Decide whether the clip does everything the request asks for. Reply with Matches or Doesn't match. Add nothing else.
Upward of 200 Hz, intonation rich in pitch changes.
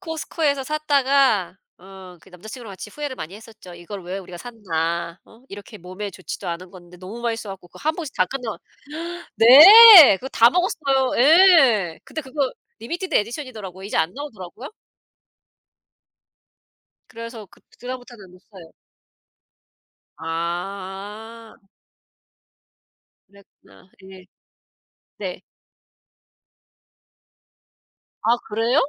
Matches